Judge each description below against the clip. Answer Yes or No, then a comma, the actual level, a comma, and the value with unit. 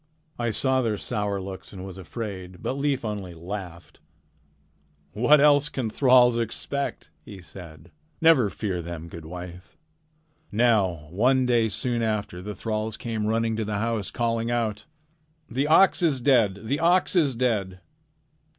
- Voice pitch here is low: Yes, low, 110 Hz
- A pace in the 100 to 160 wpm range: Yes, average, 150 wpm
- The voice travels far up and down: No, average, 4.7 semitones